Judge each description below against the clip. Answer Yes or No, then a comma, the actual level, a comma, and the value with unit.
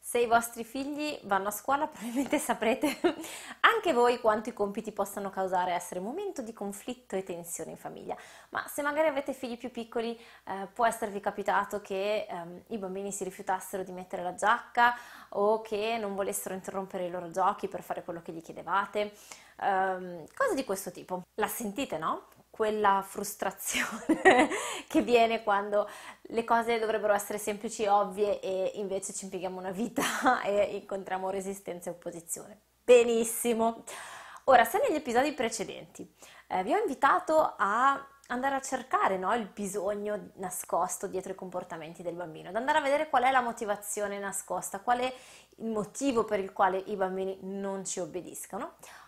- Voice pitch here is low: No, high, 205 Hz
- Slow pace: No, average, 165 wpm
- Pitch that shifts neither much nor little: Yes, average, 3.8 semitones